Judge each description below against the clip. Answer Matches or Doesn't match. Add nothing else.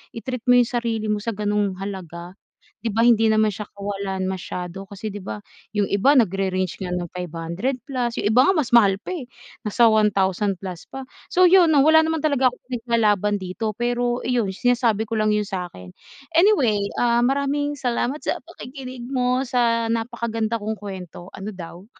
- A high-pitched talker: Matches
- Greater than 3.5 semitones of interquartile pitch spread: Matches